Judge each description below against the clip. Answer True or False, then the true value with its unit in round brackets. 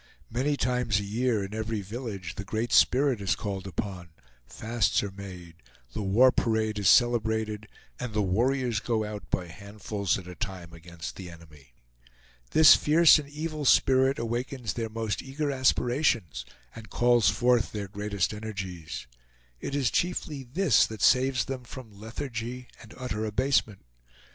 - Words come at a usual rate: True (155 wpm)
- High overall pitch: False (110 Hz)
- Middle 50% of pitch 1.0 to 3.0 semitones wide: False (4.2 semitones)